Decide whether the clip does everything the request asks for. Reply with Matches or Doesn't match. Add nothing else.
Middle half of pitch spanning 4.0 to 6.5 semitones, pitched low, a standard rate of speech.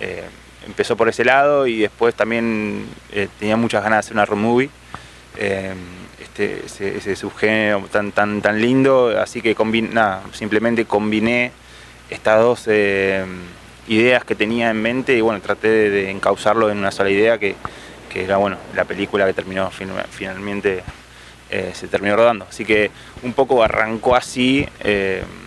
Doesn't match